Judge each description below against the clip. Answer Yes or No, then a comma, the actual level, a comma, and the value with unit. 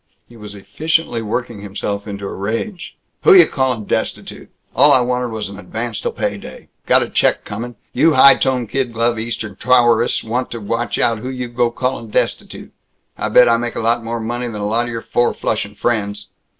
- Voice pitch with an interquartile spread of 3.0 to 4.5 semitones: No, narrow, 2.6 semitones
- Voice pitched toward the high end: No, low, 115 Hz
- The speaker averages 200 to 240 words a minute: Yes, fast, 205 wpm